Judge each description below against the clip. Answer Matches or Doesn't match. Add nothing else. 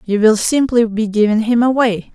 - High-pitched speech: Matches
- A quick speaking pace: Doesn't match